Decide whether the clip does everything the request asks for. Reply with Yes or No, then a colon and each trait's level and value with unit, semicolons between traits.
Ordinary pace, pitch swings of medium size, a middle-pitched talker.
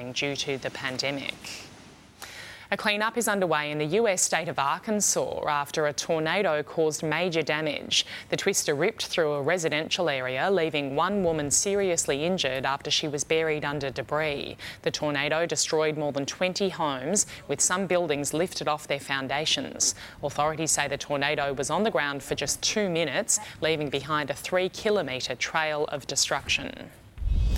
Yes: average, 155 wpm; average, 3.3 semitones; medium, 150 Hz